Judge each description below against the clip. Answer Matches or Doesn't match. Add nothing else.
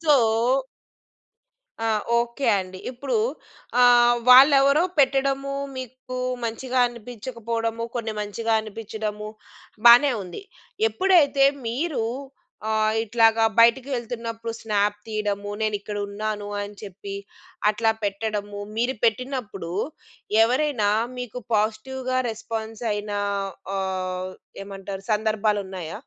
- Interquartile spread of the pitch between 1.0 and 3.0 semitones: Doesn't match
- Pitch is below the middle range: Doesn't match